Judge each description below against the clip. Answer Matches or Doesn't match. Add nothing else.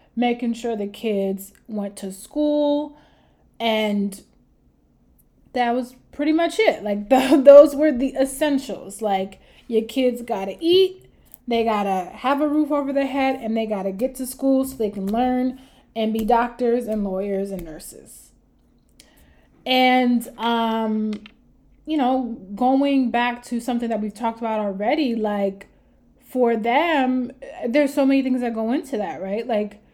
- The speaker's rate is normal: Matches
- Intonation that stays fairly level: Doesn't match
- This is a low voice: Doesn't match